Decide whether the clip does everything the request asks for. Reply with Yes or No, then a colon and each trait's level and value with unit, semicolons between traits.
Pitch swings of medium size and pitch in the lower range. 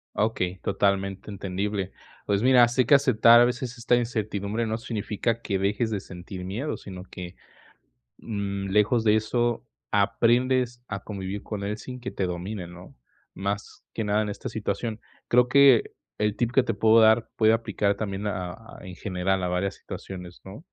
Yes: average, 3.2 semitones; low, 105 Hz